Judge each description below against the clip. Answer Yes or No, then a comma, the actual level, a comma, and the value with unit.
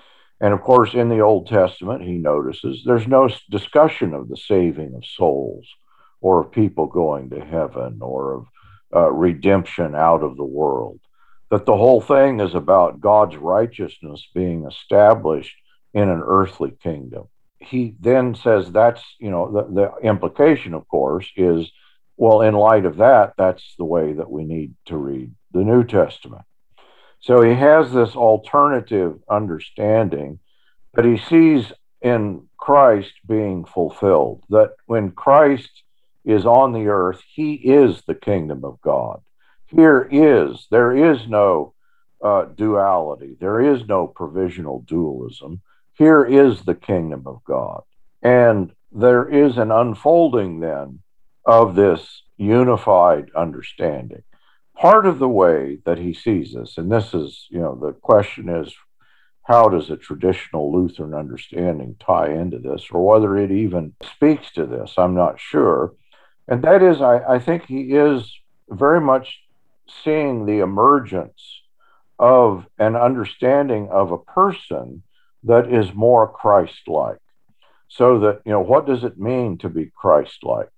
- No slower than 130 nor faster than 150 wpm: Yes, average, 145 wpm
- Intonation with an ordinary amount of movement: No, wide, 6.1 semitones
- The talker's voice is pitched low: Yes, low, 105 Hz